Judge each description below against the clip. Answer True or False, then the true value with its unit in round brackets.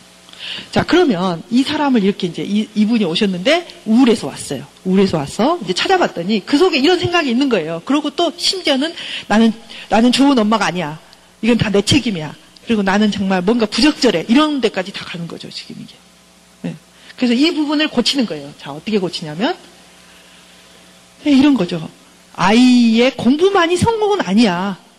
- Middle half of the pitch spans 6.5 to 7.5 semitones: False (8.4 semitones)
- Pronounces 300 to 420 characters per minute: True (360 characters per minute)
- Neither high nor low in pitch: False (220 Hz)